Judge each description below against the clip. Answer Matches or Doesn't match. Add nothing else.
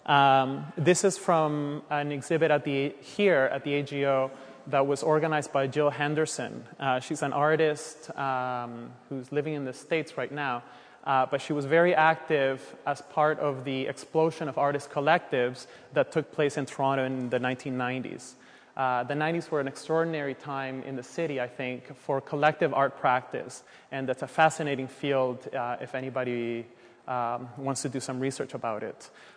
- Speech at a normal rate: Matches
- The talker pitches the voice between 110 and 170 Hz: Matches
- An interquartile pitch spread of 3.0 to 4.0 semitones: Doesn't match